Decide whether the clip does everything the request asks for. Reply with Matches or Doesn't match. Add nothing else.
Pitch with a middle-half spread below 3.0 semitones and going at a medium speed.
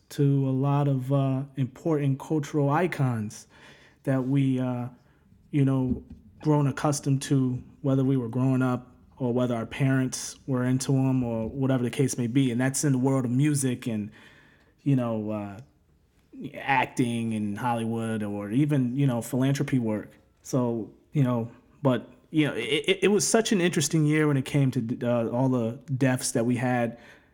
Matches